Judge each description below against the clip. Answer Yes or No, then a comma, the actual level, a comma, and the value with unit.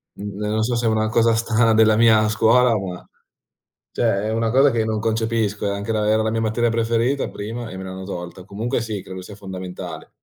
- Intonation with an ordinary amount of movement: No, narrow, 2.1 semitones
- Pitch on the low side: Yes, low, 110 Hz